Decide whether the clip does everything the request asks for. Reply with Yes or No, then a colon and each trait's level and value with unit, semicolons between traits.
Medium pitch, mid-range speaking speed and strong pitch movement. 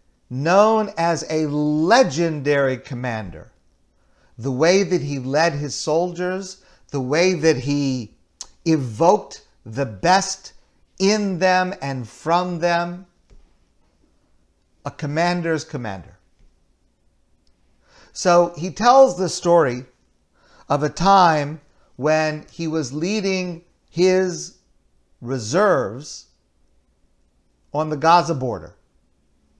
No: medium, 155 Hz; slow, 90 wpm; wide, 6.1 semitones